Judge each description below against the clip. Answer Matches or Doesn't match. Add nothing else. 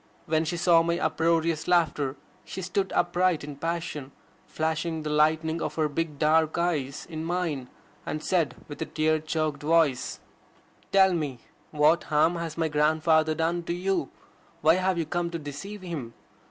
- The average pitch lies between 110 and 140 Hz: Doesn't match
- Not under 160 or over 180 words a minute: Matches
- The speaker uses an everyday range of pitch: Doesn't match